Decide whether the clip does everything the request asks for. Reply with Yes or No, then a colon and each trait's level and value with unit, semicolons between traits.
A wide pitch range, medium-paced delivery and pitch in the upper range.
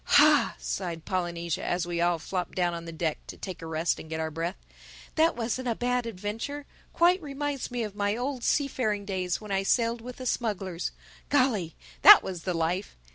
Yes: wide, 6.2 semitones; average, 185 wpm; high, 195 Hz